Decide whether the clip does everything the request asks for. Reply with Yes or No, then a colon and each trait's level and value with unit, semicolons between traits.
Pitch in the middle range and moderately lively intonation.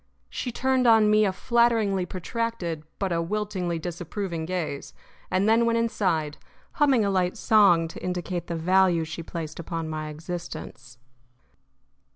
Yes: medium, 180 Hz; average, 4.3 semitones